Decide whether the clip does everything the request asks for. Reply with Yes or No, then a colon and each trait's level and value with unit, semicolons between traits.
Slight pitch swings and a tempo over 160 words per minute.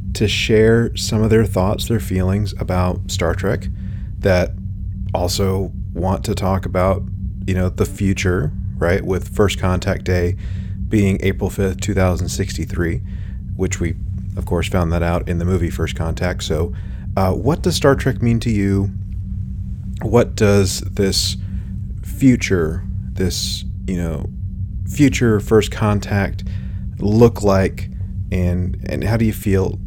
No: narrow, 1.1 semitones; average, 145 wpm